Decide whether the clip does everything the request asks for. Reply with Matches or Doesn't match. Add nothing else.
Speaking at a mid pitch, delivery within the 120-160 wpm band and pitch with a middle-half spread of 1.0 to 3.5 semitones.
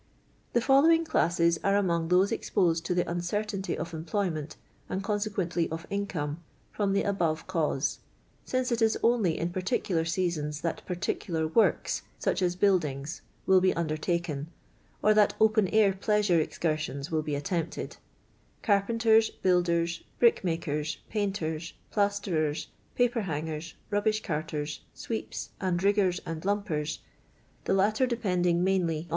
Doesn't match